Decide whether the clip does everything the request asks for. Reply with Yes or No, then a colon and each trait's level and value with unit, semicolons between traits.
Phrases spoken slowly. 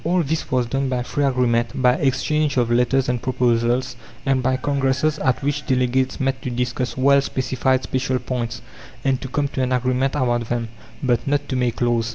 No: average, 195 wpm